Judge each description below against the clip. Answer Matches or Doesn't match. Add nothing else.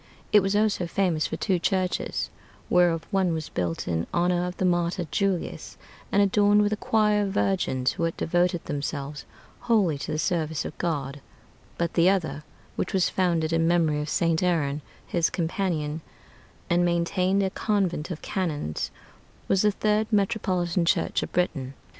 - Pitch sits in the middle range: Matches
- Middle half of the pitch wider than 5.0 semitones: Doesn't match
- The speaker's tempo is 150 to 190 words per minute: Matches